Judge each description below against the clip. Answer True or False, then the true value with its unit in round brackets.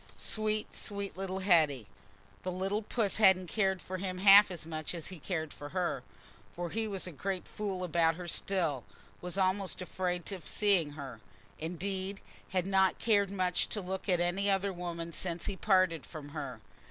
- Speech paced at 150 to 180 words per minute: True (165 wpm)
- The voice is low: False (185 Hz)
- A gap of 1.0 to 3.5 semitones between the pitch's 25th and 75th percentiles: True (2.7 semitones)